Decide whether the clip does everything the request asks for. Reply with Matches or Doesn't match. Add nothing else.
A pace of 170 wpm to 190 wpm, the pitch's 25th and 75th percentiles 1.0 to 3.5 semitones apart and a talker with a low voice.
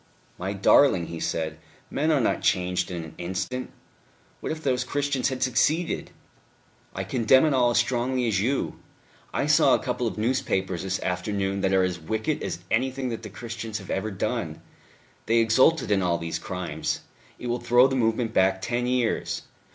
Doesn't match